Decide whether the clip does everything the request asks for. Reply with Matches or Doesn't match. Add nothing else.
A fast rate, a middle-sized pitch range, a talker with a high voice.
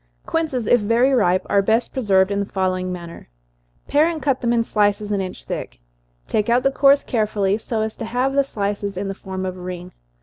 Matches